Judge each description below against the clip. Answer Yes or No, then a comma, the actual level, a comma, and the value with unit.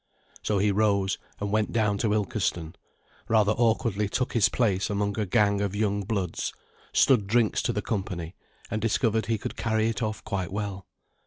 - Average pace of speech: Yes, average, 175 wpm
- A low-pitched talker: Yes, low, 105 Hz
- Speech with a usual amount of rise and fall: No, narrow, 1.7 semitones